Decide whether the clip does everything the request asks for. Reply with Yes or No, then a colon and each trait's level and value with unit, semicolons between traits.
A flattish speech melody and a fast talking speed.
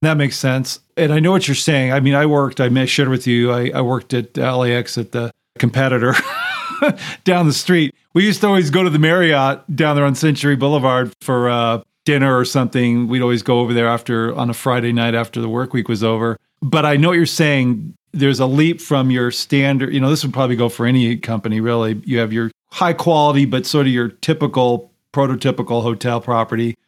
No: average, 3.5 semitones; fast, 215 wpm